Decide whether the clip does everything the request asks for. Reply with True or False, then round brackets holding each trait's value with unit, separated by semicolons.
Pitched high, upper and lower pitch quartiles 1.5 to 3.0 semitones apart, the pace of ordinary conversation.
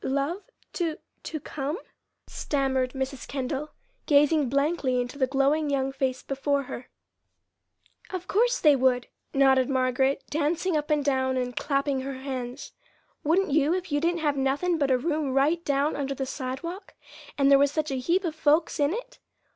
True (280 Hz; 2.7 semitones; 170 wpm)